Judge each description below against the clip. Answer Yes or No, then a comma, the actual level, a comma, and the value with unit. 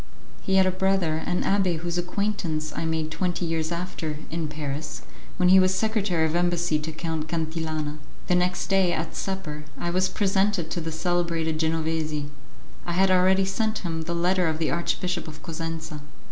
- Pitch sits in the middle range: Yes, medium, 170 Hz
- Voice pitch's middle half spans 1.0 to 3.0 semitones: Yes, narrow, 2.6 semitones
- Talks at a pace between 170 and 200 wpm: Yes, average, 175 wpm